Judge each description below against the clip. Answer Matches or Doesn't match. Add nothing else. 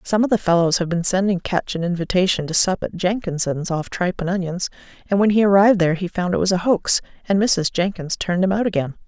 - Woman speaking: Matches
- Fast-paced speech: Matches